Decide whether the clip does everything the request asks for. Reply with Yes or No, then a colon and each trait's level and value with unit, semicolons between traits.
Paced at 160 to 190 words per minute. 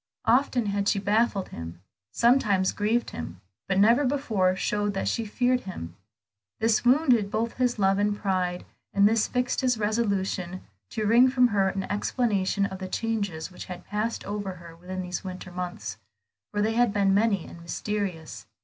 Yes: average, 170 wpm